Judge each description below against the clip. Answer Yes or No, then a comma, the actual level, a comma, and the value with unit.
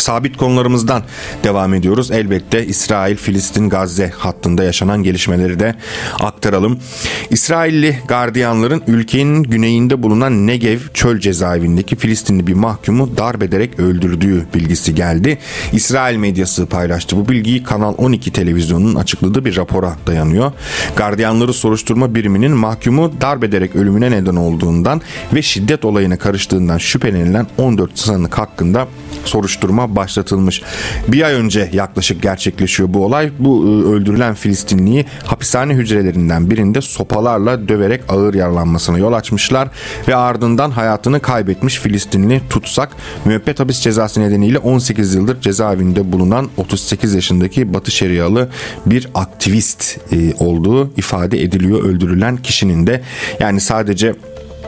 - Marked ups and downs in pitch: No, average, 4.2 semitones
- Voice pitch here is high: No, low, 105 Hz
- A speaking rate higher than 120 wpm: No, average, 115 wpm